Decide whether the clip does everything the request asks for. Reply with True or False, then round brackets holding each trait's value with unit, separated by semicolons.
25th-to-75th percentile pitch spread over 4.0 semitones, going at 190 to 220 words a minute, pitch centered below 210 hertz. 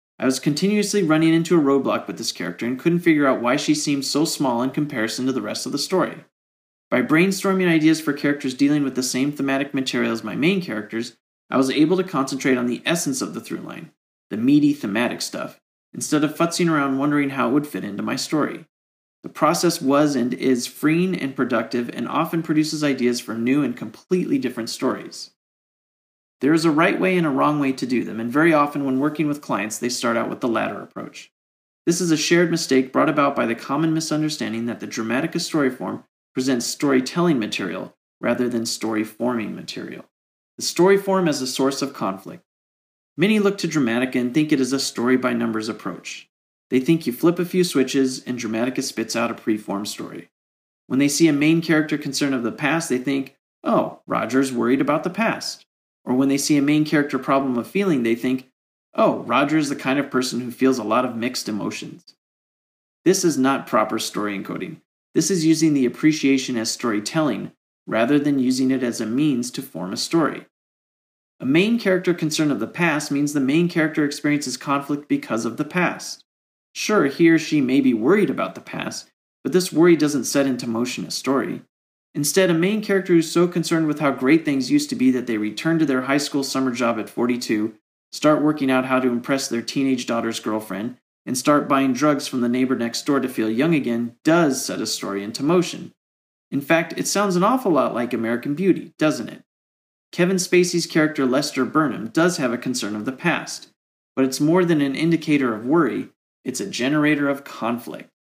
True (4.7 semitones; 205 wpm; 140 Hz)